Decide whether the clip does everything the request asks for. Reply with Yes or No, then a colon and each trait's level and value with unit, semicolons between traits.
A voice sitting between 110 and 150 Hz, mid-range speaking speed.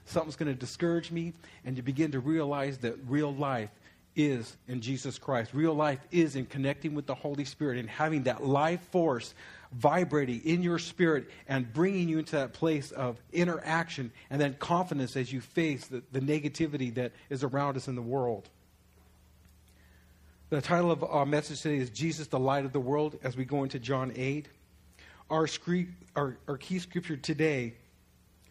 Yes: medium, 140 Hz; average, 180 wpm